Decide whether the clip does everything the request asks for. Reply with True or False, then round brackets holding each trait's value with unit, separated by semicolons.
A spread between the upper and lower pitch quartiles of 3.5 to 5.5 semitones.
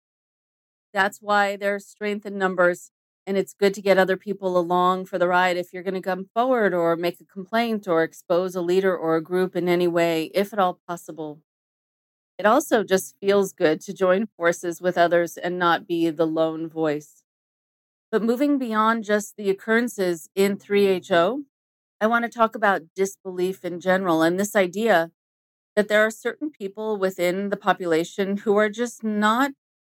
False (3.0 semitones)